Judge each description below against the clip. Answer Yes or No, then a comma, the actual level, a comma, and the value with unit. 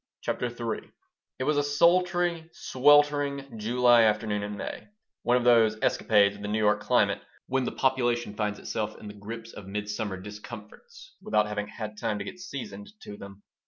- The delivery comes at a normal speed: Yes, average, 175 wpm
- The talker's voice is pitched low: Yes, low, 115 Hz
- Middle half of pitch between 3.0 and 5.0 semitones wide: No, wide, 5.5 semitones